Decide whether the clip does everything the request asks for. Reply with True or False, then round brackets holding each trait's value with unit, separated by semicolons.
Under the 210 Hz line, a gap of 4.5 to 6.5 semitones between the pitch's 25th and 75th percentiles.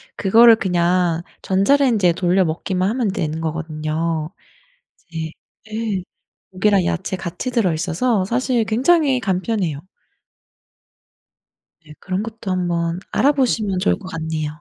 True (185 Hz; 5.1 semitones)